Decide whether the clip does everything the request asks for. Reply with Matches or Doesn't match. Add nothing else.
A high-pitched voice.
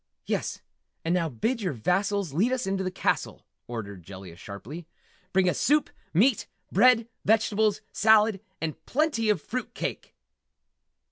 Matches